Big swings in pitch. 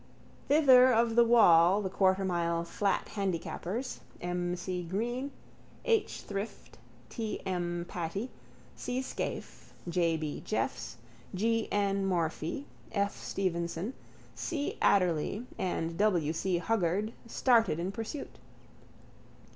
No: average, 4.7 semitones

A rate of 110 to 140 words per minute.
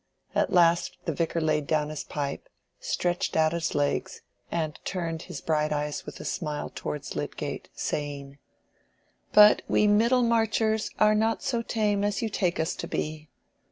No: average, 155 wpm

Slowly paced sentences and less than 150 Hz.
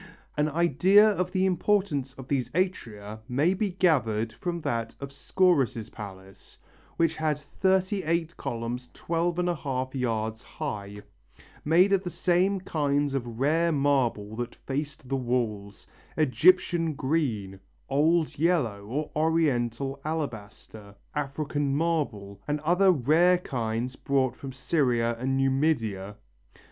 Yes: slow, 120 wpm; medium, 140 Hz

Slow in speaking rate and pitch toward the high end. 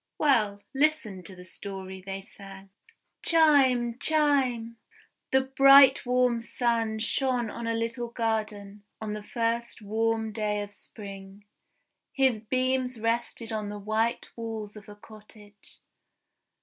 Yes: slow, 130 wpm; high, 225 Hz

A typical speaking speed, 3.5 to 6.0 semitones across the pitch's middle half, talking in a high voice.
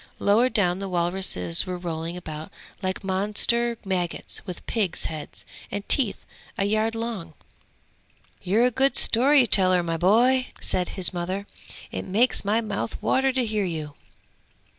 Yes: average, 145 wpm; average, 4.5 semitones; high, 195 Hz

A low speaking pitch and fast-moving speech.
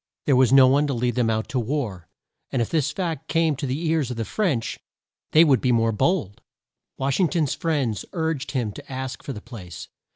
Yes: low, 130 Hz; fast, 220 wpm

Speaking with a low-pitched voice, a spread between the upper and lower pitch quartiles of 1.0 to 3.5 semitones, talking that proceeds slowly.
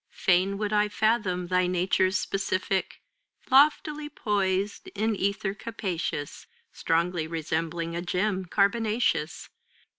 No: high, 190 Hz; average, 2.9 semitones; slow, 100 wpm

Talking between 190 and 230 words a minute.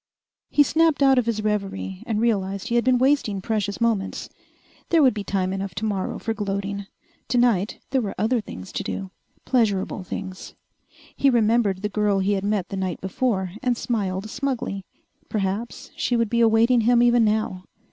No: average, 175 wpm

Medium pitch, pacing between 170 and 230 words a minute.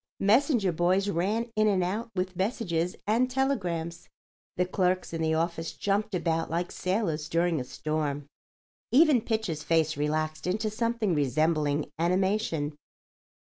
No: medium, 180 Hz; slow, 135 wpm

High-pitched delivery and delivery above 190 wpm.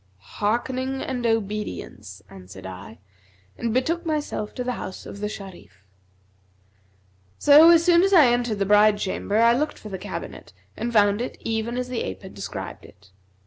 No: high, 225 Hz; average, 170 wpm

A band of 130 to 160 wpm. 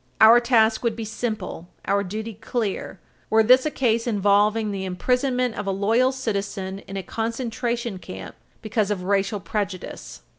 Yes: average, 155 wpm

